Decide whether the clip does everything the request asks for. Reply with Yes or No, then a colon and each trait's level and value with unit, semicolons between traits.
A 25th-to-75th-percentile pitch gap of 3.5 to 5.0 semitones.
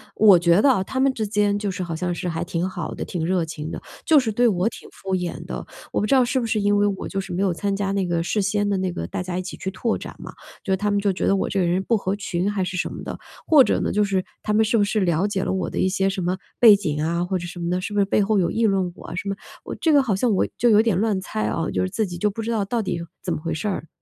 No: average, 2.9 semitones